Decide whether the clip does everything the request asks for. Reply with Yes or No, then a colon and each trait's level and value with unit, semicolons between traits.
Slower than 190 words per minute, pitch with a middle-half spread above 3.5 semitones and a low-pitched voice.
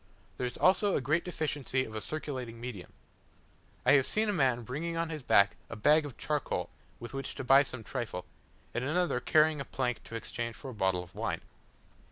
No: fast, 205 wpm; average, 4.7 semitones; low, 130 Hz